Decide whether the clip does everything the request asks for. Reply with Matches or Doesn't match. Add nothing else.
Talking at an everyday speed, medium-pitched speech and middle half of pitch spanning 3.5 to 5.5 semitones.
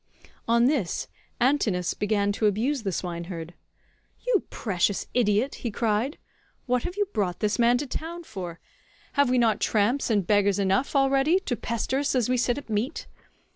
Doesn't match